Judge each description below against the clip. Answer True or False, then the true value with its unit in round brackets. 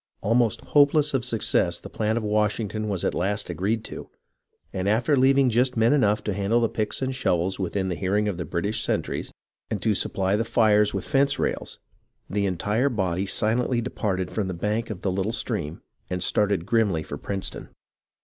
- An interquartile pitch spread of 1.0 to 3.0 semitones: False (3.5 semitones)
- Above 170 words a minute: True (190 wpm)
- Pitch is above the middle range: False (105 Hz)